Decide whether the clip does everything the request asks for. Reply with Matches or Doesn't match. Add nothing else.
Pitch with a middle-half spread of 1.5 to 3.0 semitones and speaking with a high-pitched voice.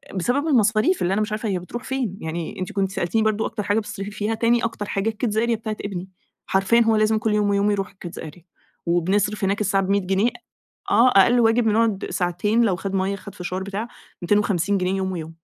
Matches